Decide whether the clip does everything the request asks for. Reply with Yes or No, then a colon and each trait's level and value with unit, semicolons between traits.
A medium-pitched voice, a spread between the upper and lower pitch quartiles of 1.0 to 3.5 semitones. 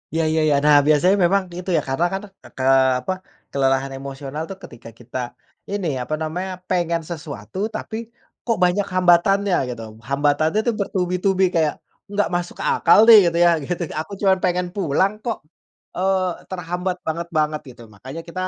No: medium, 170 Hz; average, 4.2 semitones